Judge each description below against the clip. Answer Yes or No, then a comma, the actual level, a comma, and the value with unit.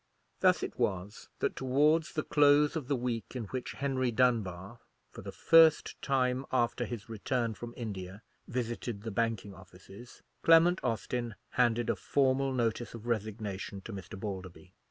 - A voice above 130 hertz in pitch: No, low, 120 Hz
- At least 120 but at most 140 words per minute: No, average, 155 wpm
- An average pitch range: Yes, average, 4.0 semitones